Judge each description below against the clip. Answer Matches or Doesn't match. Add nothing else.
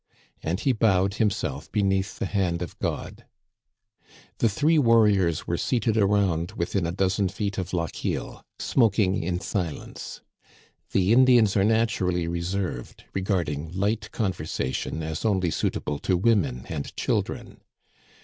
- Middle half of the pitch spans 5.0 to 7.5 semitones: Doesn't match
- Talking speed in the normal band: Doesn't match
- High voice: Doesn't match